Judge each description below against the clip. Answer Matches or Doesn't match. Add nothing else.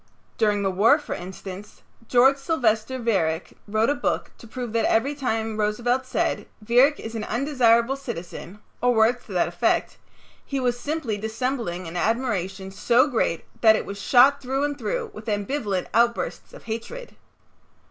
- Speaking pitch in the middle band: Doesn't match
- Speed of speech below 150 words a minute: Doesn't match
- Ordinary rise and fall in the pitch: Matches